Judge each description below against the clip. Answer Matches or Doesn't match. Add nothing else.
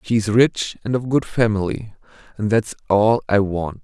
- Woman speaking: Doesn't match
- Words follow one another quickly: Doesn't match